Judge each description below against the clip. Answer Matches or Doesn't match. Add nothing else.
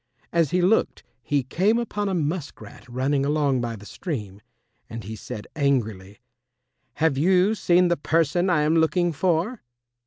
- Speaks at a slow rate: Doesn't match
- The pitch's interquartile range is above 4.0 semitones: Matches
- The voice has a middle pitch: Matches